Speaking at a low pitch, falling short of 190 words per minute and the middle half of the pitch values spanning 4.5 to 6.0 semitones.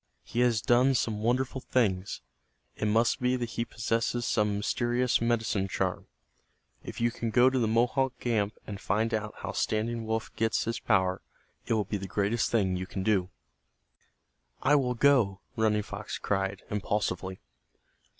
No: low, 110 Hz; average, 160 wpm; average, 2.8 semitones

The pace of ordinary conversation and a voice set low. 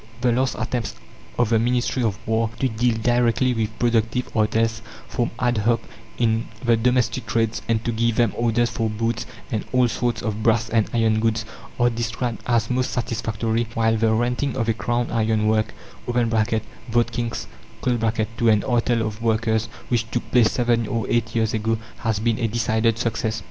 Yes: average, 175 wpm; low, 115 Hz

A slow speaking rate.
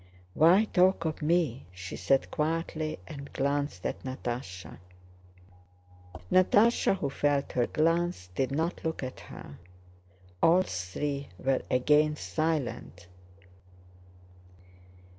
Yes: slow, 105 wpm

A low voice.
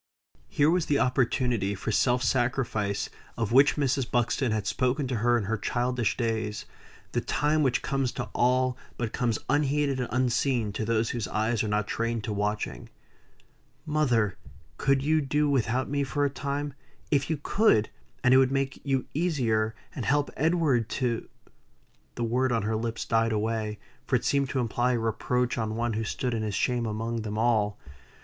Yes: low, 120 Hz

